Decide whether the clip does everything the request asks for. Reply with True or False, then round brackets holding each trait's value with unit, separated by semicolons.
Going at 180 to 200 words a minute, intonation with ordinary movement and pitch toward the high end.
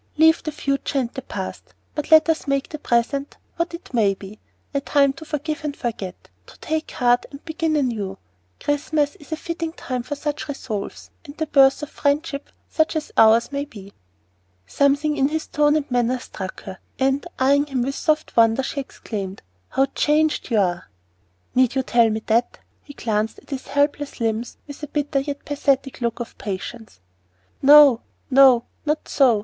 True (185 wpm; 3.9 semitones; 275 Hz)